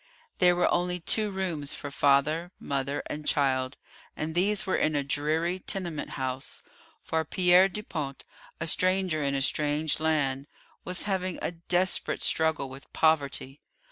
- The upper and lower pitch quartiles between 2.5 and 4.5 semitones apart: Yes, average, 4.1 semitones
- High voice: No, medium, 160 Hz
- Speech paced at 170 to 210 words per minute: No, average, 145 wpm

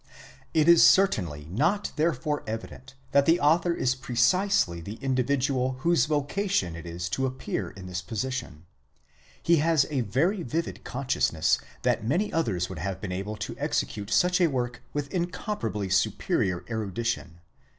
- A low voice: Yes, low, 130 Hz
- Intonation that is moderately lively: No, wide, 8.7 semitones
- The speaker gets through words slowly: No, average, 150 wpm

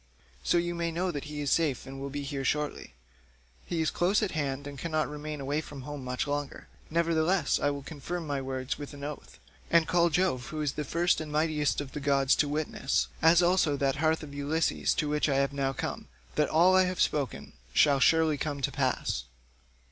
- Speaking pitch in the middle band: Yes, medium, 150 Hz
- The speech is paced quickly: Yes, fast, 210 wpm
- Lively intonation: No, narrow, 2.6 semitones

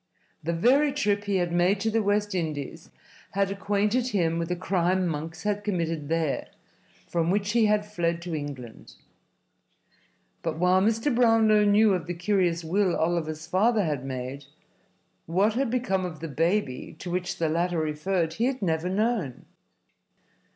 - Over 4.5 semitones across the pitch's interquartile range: No, average, 4.1 semitones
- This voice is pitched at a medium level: Yes, medium, 180 Hz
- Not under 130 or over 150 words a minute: No, average, 160 wpm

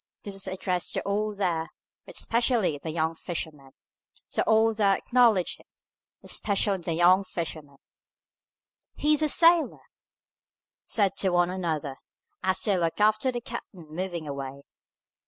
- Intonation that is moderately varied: Yes, average, 4.6 semitones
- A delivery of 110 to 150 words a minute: Yes, average, 140 wpm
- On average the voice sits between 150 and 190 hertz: Yes, medium, 185 Hz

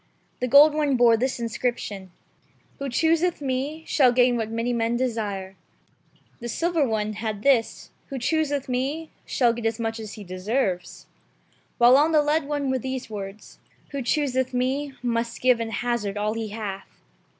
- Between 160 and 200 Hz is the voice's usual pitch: No, high, 245 Hz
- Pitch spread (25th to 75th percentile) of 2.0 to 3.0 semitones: No, average, 3.8 semitones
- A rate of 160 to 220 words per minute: Yes, average, 175 wpm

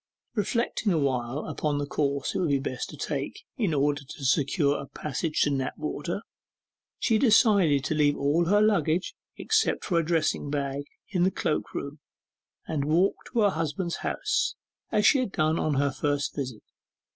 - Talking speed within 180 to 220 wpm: No, average, 170 wpm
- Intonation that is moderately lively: Yes, average, 4.7 semitones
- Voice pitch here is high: No, medium, 155 Hz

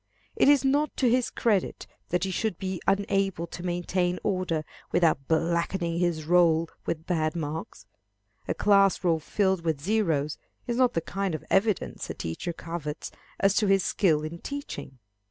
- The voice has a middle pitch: Yes, medium, 175 Hz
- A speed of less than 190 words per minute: Yes, average, 165 wpm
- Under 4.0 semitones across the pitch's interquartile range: Yes, average, 3.3 semitones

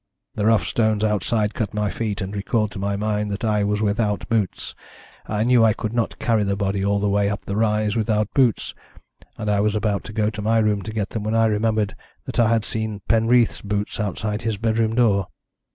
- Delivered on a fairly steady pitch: Yes, narrow, 1.5 semitones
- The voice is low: Yes, low, 105 Hz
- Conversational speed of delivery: No, fast, 220 wpm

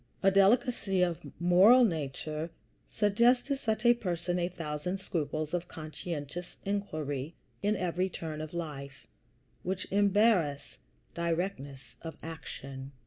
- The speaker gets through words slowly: Yes, slow, 120 wpm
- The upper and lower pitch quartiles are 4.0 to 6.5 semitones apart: Yes, average, 4.4 semitones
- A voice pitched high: No, medium, 175 Hz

